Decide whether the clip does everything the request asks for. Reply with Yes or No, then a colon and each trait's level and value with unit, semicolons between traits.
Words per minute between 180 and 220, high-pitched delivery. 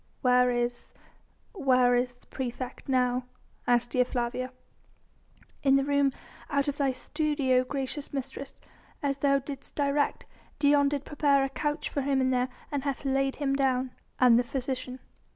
No: average, 150 wpm; very high, 270 Hz